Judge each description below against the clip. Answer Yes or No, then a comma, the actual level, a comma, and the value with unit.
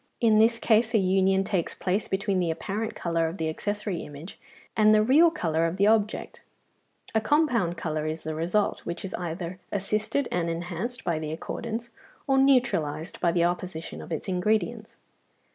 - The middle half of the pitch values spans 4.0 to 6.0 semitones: Yes, average, 4.6 semitones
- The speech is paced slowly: No, average, 175 wpm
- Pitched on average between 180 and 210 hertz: Yes, high, 190 Hz